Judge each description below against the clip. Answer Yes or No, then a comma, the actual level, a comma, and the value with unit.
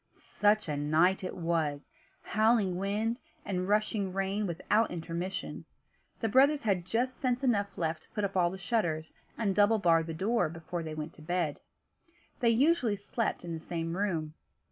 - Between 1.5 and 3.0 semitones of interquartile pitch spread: No, average, 4.6 semitones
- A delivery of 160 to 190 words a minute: Yes, average, 175 wpm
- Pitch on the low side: No, high, 190 Hz